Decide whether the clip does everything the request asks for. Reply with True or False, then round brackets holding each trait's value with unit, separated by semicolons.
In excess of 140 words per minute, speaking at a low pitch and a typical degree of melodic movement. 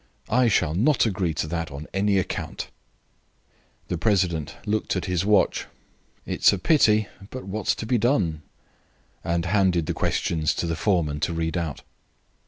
True (165 wpm; 90 Hz; 4.4 semitones)